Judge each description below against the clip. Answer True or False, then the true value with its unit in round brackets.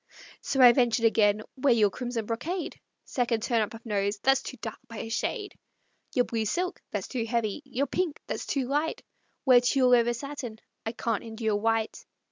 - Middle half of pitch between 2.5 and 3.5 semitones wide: True (3.0 semitones)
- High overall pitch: True (235 Hz)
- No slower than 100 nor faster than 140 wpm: False (185 wpm)